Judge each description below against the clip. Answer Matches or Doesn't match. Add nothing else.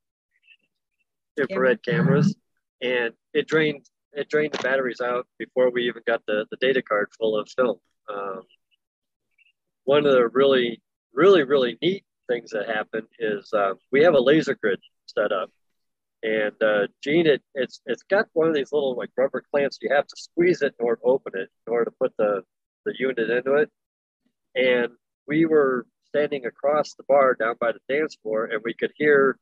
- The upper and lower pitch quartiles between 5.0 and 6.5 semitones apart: Matches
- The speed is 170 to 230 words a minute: Matches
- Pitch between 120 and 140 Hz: Matches